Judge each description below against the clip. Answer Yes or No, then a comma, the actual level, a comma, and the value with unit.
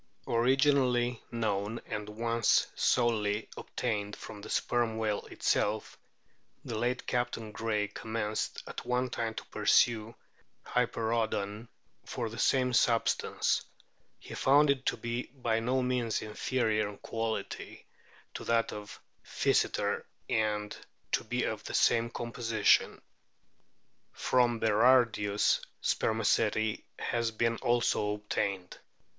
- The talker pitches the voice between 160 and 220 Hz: No, low, 115 Hz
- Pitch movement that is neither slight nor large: No, narrow, 2.1 semitones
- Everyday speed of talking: No, slow, 115 wpm